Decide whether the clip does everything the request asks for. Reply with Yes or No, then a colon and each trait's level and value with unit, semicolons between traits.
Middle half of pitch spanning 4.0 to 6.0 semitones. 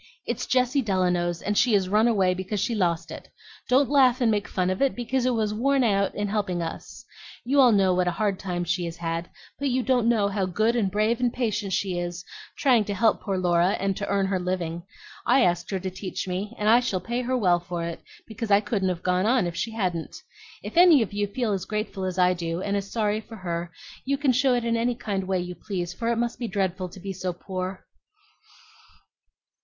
Yes: average, 4.3 semitones